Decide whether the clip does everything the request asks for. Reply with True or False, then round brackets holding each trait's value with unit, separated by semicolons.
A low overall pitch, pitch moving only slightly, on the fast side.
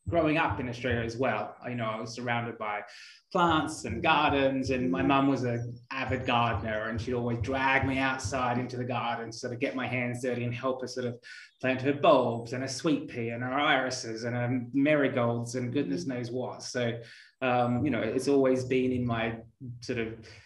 True (125 Hz; 2.0 semitones; 210 wpm)